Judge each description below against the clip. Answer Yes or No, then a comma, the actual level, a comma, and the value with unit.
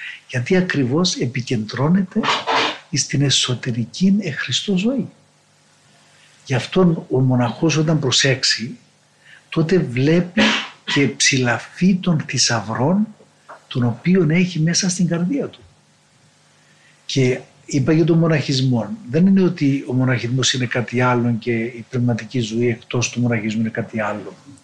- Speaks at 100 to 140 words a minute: Yes, average, 120 wpm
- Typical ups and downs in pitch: No, wide, 5.7 semitones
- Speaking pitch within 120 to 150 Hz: Yes, low, 135 Hz